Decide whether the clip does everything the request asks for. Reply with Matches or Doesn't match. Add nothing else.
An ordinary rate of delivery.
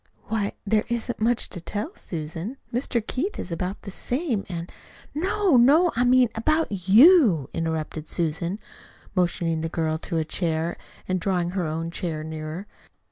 Matches